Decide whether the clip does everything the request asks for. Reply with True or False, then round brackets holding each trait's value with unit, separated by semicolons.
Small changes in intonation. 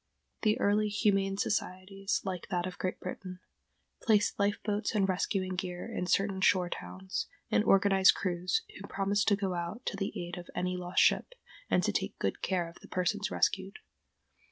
True (1.9 semitones)